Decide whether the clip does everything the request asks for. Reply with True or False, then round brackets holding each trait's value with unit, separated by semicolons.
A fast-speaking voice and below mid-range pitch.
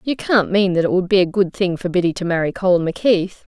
False (270 wpm; 185 Hz)